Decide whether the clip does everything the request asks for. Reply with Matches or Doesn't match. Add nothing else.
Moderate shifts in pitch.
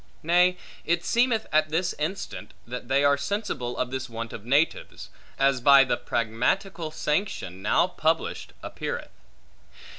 Doesn't match